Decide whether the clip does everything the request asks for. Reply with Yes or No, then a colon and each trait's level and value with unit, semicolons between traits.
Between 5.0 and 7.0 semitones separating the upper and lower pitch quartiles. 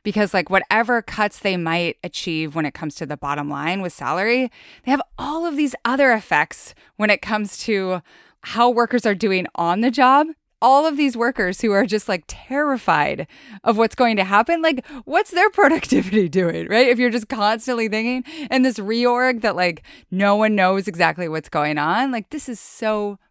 Yes: average, 5.3 semitones